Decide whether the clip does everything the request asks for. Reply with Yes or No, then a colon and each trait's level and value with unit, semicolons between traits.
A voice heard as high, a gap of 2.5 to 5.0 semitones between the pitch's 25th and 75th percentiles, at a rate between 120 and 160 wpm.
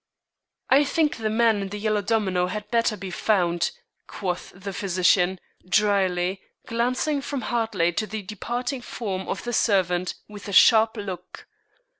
Yes: high, 205 Hz; average, 3.6 semitones; average, 150 wpm